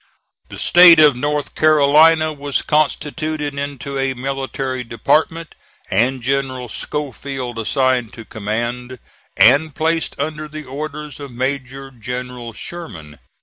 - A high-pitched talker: No, low, 135 Hz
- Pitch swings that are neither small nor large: Yes, average, 3.3 semitones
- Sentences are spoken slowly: Yes, slow, 115 wpm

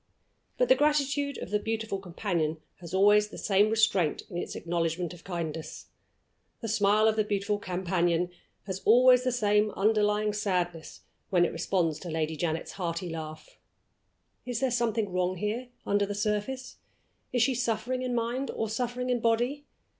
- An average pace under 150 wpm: No, average, 160 wpm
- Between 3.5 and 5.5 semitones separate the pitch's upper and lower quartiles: Yes, average, 4.7 semitones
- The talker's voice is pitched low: No, high, 210 Hz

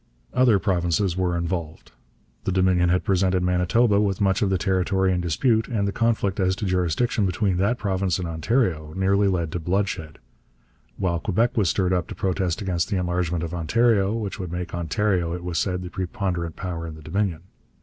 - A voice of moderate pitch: No, very low, 95 Hz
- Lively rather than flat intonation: No, narrow, 2.5 semitones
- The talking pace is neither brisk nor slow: Yes, average, 190 wpm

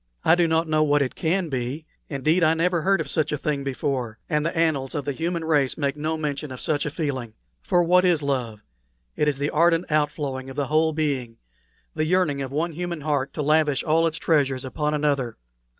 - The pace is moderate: No, fast, 215 wpm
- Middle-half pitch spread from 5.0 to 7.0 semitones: No, average, 2.7 semitones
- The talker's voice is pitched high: No, medium, 150 Hz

